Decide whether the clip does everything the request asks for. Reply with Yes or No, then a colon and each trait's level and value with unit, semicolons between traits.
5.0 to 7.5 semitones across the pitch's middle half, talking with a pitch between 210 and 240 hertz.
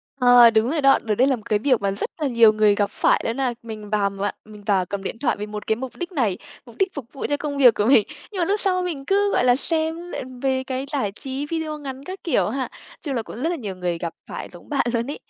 No: wide, 5.5 semitones; very high, 255 Hz